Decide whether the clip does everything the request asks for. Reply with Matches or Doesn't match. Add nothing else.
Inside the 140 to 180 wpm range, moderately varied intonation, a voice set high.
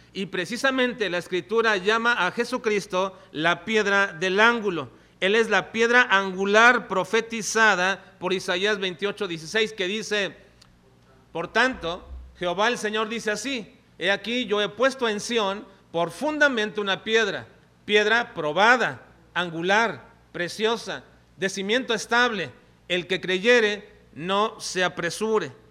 Doesn't match